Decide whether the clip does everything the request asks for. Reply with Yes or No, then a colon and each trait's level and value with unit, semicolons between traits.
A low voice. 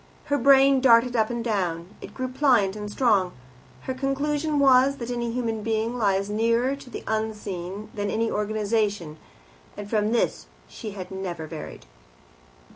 No: high, 225 Hz